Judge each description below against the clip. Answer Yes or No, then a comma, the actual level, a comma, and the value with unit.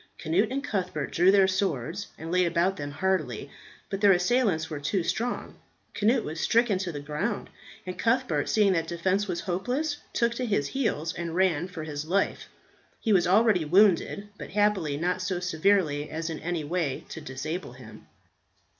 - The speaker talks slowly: No, average, 175 wpm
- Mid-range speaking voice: Yes, medium, 180 Hz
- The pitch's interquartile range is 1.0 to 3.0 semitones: No, average, 4.2 semitones